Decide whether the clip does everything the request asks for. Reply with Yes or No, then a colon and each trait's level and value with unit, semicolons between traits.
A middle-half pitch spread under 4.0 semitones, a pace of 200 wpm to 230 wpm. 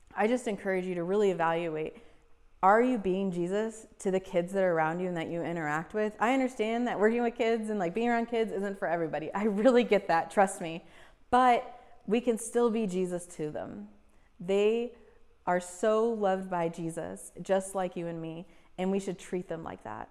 No: average, 4.5 semitones; fast, 205 wpm